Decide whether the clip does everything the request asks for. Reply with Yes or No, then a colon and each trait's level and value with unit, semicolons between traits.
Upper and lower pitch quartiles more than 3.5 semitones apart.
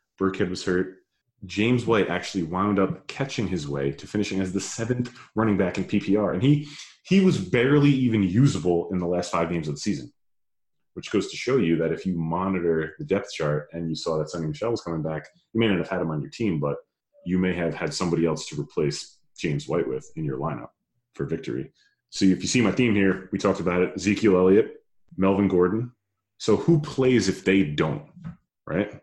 Yes: average, 4.6 semitones